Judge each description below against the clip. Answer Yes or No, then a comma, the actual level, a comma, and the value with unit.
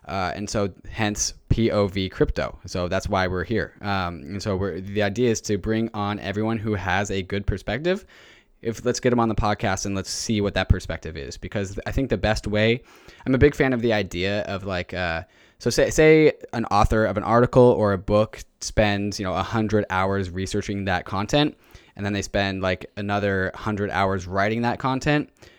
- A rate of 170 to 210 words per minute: Yes, fast, 205 wpm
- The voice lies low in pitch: Yes, low, 100 Hz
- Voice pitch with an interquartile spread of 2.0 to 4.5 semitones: Yes, average, 2.8 semitones